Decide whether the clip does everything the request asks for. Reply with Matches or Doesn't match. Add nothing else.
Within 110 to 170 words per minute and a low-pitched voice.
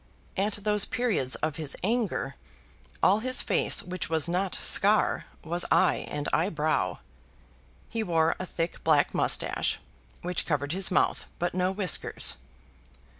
Doesn't match